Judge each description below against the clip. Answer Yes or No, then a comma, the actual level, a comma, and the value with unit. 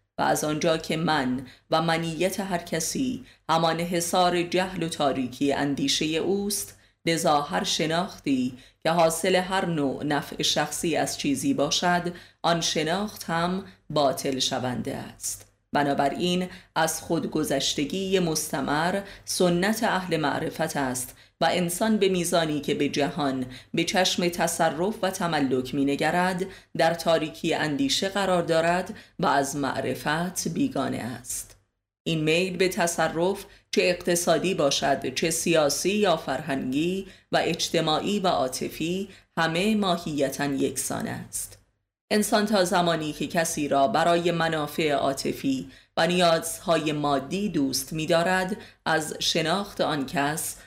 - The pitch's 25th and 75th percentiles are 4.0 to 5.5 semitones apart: Yes, average, 4.4 semitones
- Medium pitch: Yes, medium, 165 Hz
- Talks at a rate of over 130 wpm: No, average, 120 wpm